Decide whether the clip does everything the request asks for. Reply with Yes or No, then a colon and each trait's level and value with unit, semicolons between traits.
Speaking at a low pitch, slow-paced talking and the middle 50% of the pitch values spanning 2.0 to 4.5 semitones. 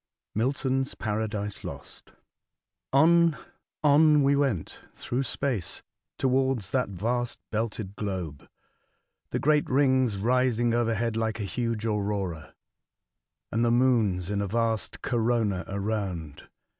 Yes: low, 115 Hz; slow, 110 wpm; average, 4.2 semitones